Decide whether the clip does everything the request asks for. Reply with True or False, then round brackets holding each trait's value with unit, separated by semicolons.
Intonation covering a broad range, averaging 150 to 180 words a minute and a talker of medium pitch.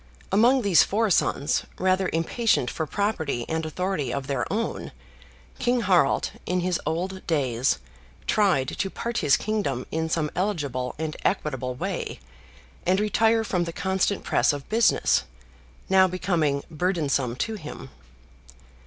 False (5.8 semitones; 135 wpm; 175 Hz)